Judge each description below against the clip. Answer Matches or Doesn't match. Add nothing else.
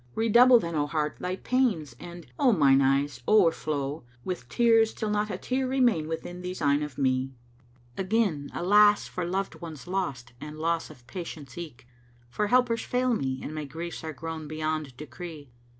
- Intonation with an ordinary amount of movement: Doesn't match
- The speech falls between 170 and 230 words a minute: Matches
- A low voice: Doesn't match